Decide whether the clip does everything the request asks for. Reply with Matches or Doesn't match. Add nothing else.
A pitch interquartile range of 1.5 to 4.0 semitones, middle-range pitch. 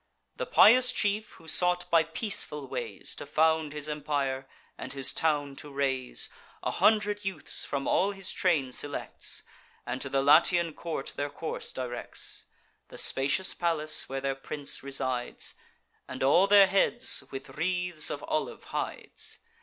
Doesn't match